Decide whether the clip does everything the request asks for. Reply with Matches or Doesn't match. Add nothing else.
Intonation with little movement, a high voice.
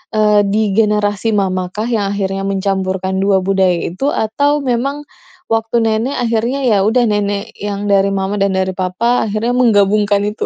Matches